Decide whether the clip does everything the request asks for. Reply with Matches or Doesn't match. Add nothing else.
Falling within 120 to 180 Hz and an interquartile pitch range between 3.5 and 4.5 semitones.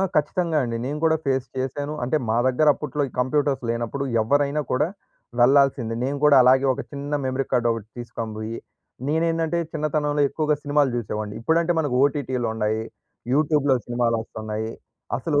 Matches